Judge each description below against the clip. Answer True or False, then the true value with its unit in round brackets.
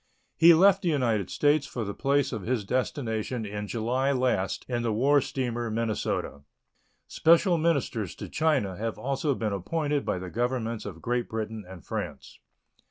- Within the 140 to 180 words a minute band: True (165 wpm)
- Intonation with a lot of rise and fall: False (4.6 semitones)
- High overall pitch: False (120 Hz)